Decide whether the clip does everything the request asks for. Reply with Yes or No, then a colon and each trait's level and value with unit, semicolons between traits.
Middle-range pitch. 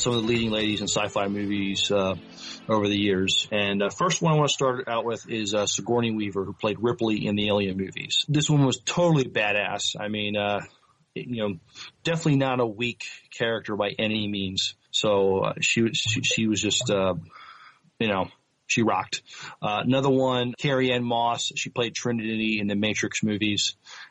No: low, 110 Hz